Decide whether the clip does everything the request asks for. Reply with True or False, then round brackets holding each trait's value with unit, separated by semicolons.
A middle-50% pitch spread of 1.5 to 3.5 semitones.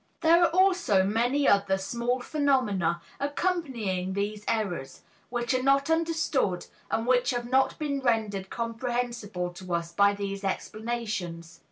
False (5.5 semitones)